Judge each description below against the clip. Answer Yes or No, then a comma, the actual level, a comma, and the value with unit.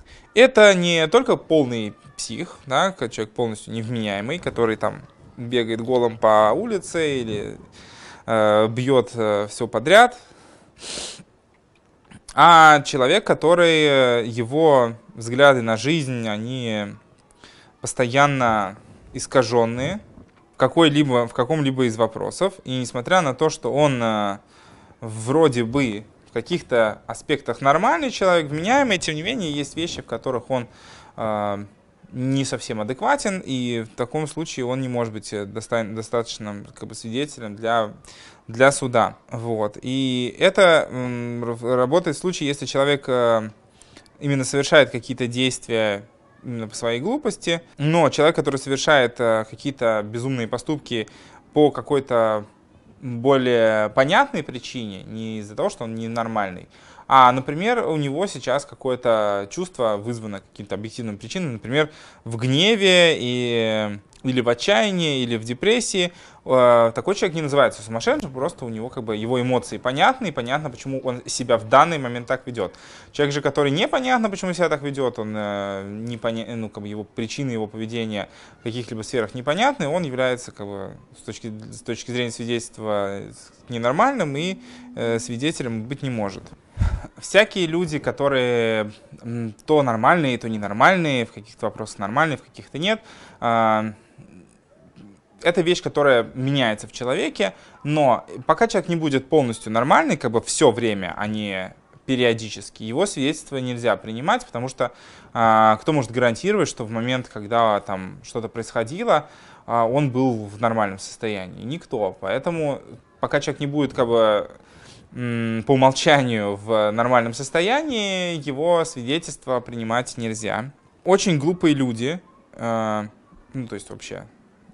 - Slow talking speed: No, average, 135 wpm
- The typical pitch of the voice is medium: No, low, 125 Hz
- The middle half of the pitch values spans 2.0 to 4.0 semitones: No, average, 4.6 semitones